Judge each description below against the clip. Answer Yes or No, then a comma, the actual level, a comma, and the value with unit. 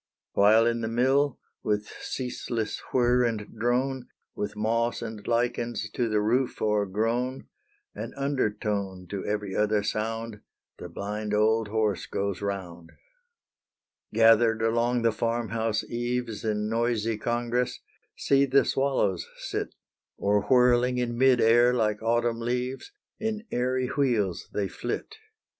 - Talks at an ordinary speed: No, slow, 130 wpm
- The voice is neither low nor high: No, low, 115 Hz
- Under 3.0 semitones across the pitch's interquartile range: Yes, narrow, 2.6 semitones